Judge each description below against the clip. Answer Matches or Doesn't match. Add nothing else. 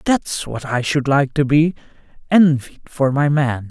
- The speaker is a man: Matches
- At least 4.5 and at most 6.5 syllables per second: Doesn't match